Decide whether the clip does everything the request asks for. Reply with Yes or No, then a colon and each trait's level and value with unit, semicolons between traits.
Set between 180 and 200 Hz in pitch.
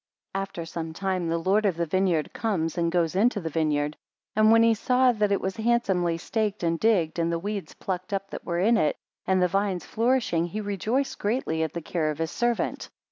Yes: high, 190 Hz